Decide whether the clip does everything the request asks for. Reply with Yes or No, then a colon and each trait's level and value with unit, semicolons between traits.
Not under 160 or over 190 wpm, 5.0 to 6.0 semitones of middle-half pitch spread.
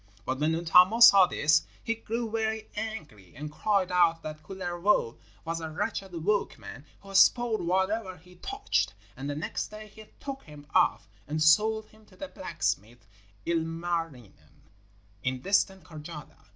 No: average, 150 wpm; wide, 5.5 semitones